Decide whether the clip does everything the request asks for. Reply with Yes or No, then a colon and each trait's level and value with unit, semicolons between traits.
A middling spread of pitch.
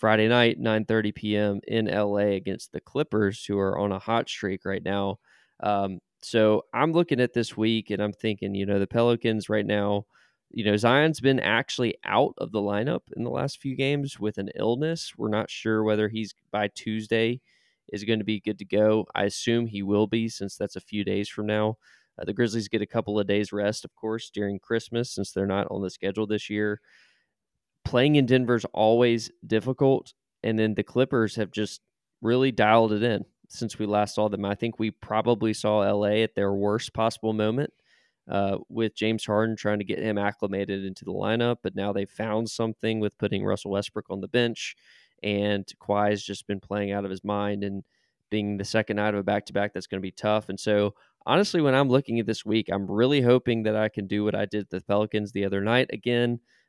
No: narrow, 2.0 semitones